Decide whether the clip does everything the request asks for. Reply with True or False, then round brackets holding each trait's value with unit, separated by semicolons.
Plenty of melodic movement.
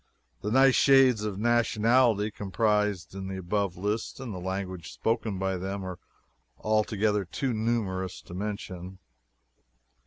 False (3.1 semitones)